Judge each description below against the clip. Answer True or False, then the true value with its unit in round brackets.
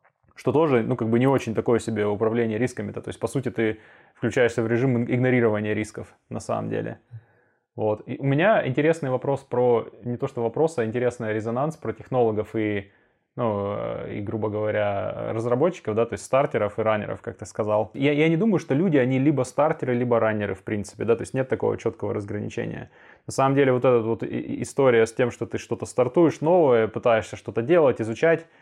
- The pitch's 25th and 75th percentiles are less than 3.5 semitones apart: True (3.0 semitones)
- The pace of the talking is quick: True (195 wpm)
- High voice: False (120 Hz)